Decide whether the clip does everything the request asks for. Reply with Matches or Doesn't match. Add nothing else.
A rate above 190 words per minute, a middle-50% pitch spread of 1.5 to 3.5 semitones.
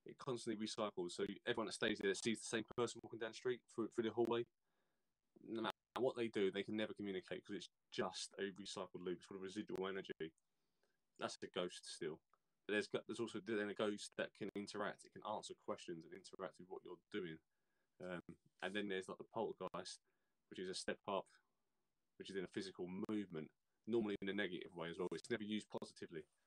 Matches